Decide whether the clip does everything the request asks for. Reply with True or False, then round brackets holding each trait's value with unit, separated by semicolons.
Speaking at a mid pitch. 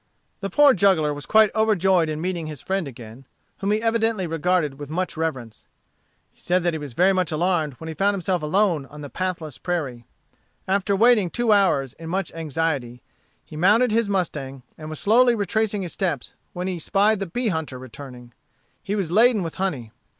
True (175 Hz)